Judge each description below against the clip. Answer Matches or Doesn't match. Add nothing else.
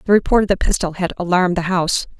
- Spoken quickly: Matches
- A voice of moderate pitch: Matches